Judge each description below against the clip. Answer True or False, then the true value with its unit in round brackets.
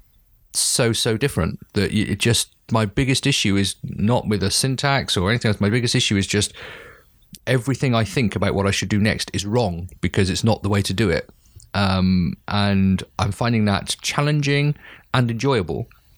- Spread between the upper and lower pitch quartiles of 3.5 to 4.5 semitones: True (3.8 semitones)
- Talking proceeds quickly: False (180 wpm)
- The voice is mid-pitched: False (105 Hz)